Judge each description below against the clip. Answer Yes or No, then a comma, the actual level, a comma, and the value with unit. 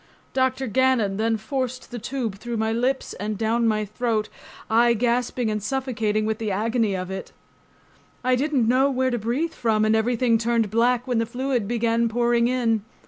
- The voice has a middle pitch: No, high, 235 Hz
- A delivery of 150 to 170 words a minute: No, average, 180 wpm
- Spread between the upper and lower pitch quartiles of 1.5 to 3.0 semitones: Yes, narrow, 2.5 semitones